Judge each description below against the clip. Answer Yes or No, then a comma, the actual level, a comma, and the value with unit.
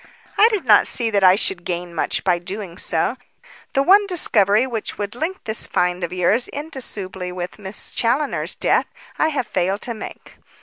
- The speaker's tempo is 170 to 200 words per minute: Yes, average, 180 wpm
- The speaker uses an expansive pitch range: Yes, wide, 6.3 semitones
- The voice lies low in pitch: No, high, 210 Hz